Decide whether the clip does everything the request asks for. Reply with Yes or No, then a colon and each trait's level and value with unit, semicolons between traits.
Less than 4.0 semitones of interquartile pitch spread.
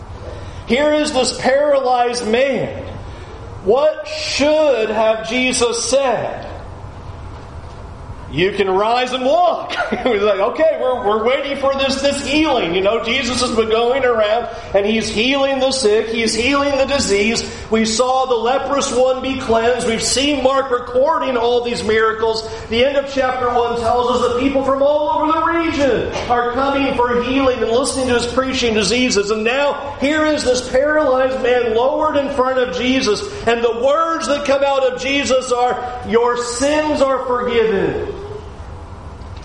Yes: average, 3.5 semitones